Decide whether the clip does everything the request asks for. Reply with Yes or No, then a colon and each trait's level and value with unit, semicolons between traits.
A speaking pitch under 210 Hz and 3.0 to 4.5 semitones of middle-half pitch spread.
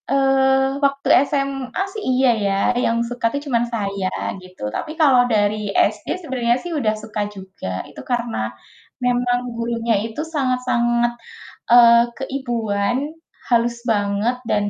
No: high, 240 Hz; average, 3.3 semitones